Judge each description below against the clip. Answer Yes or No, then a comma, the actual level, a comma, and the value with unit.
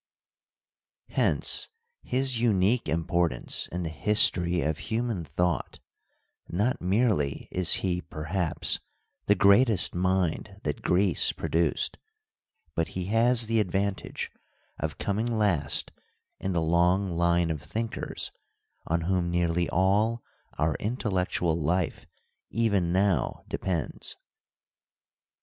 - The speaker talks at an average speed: No, slow, 105 wpm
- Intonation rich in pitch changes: No, average, 3.5 semitones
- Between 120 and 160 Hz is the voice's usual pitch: No, very low, 90 Hz